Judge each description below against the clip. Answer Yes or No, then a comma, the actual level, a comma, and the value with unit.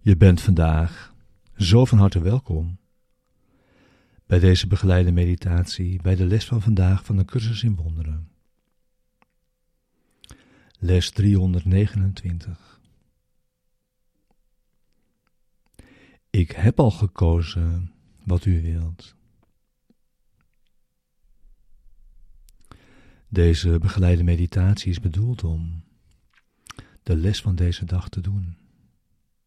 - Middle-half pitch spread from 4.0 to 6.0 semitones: No, average, 2.8 semitones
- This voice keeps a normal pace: No, slow, 90 wpm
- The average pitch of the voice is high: No, very low, 90 Hz